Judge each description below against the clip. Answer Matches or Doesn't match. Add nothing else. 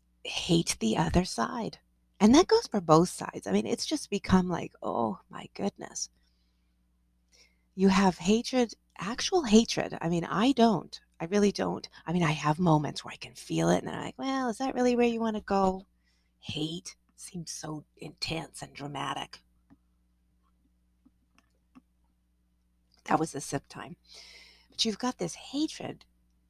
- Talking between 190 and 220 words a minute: Doesn't match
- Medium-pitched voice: Matches